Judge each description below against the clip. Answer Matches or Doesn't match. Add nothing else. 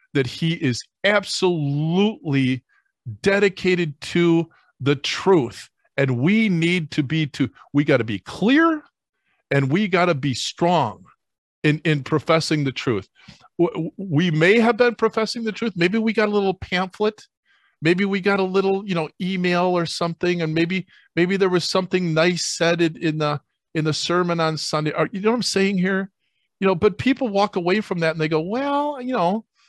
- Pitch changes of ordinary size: Matches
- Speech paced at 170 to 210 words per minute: Matches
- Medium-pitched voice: Matches